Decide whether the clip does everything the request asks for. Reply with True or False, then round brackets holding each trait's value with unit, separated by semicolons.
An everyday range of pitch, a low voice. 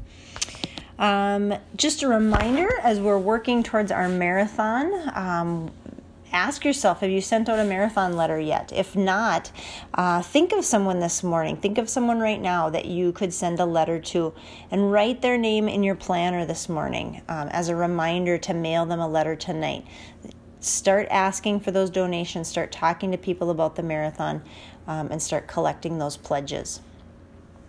False (4.0 semitones; 180 Hz)